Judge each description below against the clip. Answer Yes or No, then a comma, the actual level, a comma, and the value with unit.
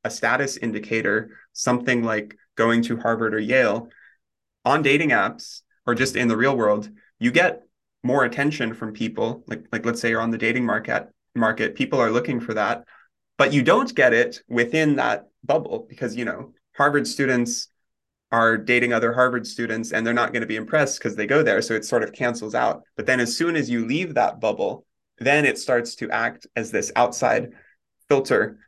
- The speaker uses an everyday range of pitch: No, narrow, 1.8 semitones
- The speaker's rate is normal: Yes, average, 195 wpm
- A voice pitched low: Yes, low, 115 Hz